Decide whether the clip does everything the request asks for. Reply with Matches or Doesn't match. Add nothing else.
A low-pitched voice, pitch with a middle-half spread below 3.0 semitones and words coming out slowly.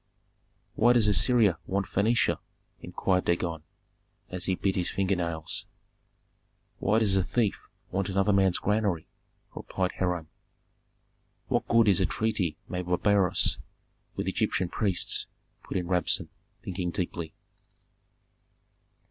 Matches